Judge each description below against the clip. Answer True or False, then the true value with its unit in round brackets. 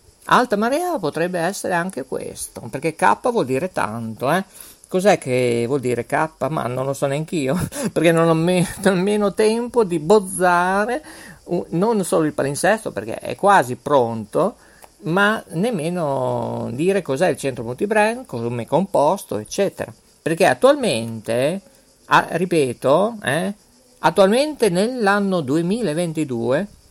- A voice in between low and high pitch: True (170 Hz)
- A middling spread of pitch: False (7.2 semitones)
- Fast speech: False (130 wpm)